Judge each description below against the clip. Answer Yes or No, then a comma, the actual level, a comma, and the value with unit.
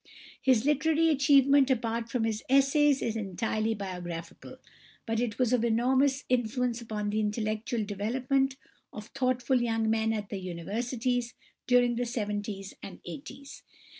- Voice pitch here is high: Yes, high, 235 Hz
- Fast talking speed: No, slow, 135 wpm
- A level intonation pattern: No, average, 3.5 semitones